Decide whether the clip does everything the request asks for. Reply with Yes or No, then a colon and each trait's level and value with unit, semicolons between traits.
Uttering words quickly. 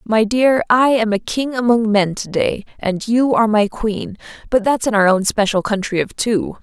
Yes: fast, 215 wpm